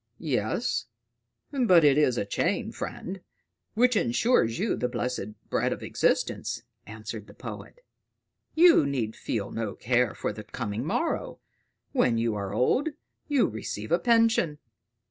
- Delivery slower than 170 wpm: Yes, average, 140 wpm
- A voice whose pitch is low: Yes, low, 125 Hz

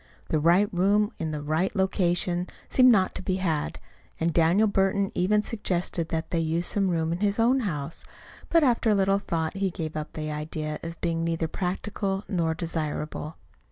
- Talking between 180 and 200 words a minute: Yes, average, 185 wpm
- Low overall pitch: No, medium, 175 Hz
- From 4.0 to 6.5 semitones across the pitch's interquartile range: No, average, 3.5 semitones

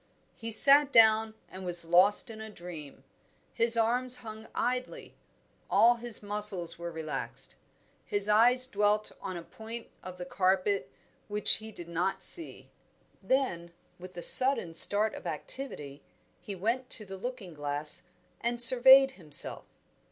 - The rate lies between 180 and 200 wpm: No, average, 145 wpm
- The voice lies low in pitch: No, high, 210 Hz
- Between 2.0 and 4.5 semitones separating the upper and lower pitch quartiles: No, average, 5.1 semitones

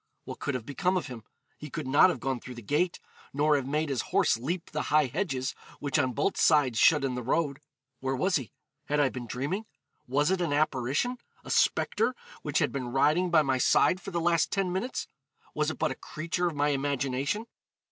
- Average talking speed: No, fast, 215 wpm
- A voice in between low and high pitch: Yes, medium, 145 Hz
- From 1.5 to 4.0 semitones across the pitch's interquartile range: No, average, 4.4 semitones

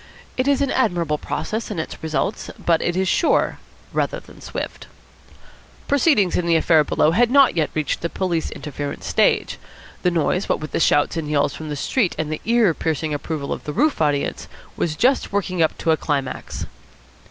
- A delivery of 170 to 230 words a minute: Yes, average, 190 wpm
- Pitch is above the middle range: No, medium, 165 Hz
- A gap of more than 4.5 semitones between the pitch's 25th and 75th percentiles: Yes, average, 5.2 semitones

